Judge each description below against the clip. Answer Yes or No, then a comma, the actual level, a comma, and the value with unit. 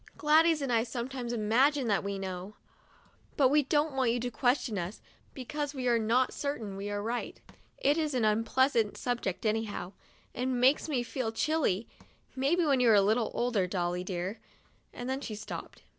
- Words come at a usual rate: Yes, average, 190 wpm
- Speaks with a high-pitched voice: Yes, high, 240 Hz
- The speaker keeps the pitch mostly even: No, average, 4.3 semitones